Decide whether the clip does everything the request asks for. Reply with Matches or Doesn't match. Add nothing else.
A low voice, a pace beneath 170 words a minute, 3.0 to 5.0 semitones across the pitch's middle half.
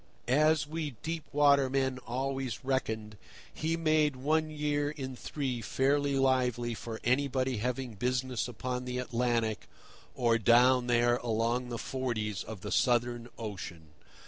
Doesn't match